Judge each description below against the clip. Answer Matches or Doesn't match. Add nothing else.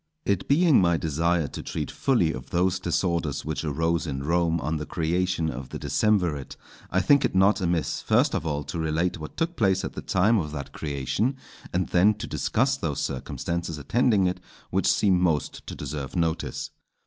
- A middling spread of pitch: Matches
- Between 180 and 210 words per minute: Matches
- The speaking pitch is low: Matches